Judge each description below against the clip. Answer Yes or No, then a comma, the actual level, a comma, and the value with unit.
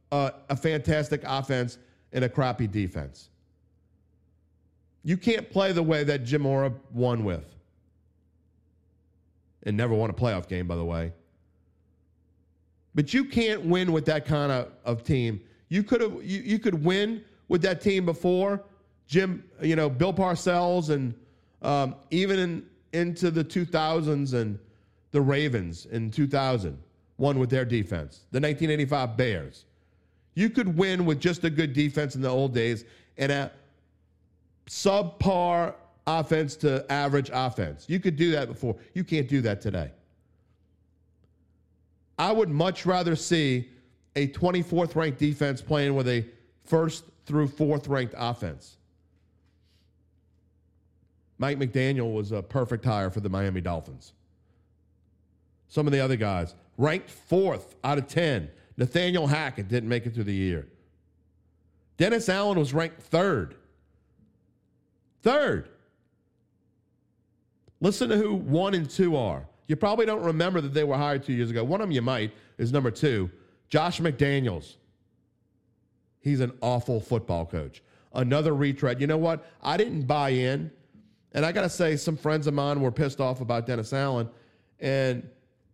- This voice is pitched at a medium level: No, low, 130 Hz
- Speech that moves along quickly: No, average, 150 wpm